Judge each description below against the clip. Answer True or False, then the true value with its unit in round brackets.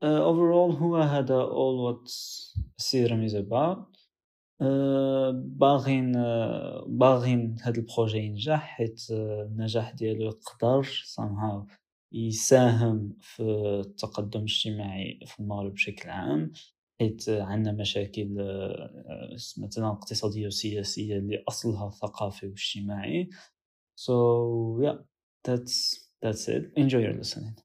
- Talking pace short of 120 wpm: True (100 wpm)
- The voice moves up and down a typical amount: True (3.7 semitones)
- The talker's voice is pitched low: True (115 Hz)